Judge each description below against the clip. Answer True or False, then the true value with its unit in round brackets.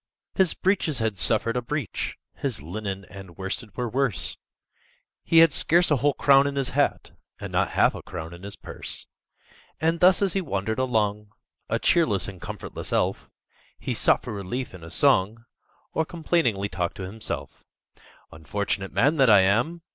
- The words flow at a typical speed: True (170 wpm)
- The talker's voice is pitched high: False (110 Hz)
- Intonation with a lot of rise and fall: True (7.1 semitones)